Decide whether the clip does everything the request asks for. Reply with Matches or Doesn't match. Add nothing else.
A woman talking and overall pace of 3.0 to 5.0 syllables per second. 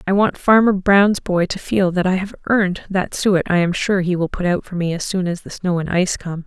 Doesn't match